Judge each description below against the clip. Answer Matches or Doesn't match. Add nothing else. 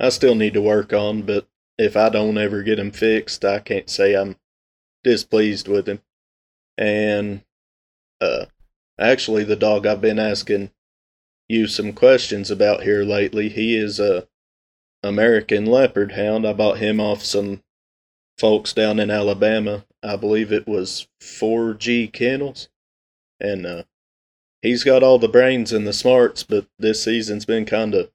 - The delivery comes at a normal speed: Matches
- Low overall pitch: Matches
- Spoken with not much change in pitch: Matches